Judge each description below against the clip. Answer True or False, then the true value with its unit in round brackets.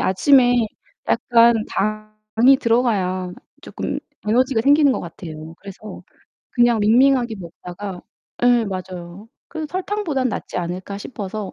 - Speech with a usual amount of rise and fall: True (5.0 semitones)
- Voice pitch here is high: True (215 Hz)